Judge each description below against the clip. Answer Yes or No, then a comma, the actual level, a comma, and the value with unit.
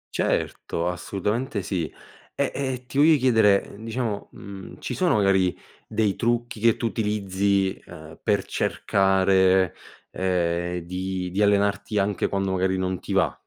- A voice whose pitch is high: No, low, 100 Hz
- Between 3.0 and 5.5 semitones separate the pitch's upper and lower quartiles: No, narrow, 2.6 semitones